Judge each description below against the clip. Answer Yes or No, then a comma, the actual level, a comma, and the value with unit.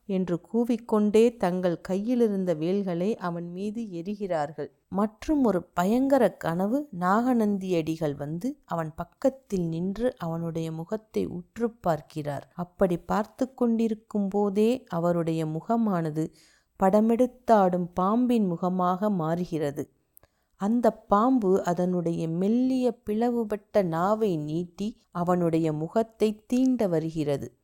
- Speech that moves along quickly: No, average, 90 wpm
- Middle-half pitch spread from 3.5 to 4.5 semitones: No, average, 4.9 semitones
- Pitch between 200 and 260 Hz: No, high, 190 Hz